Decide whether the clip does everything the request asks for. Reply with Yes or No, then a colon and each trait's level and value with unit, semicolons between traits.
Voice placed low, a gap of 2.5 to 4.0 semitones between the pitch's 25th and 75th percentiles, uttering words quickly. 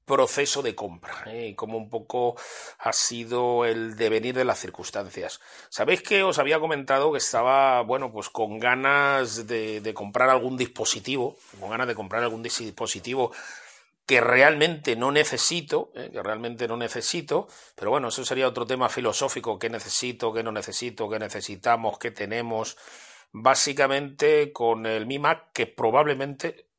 No: low, 120 Hz; average, 3.6 semitones; average, 155 wpm